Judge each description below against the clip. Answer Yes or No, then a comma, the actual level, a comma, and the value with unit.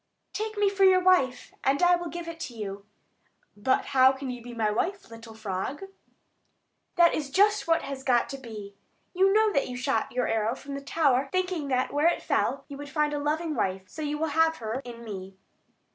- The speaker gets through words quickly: Yes, fast, 215 wpm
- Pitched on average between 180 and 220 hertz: No, very high, 275 Hz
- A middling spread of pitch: No, wide, 6.1 semitones